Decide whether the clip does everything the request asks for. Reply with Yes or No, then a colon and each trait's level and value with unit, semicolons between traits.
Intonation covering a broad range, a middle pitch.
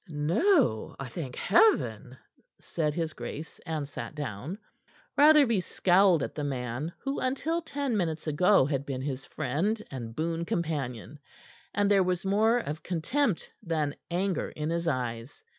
Yes: wide, 5.9 semitones; medium, 165 Hz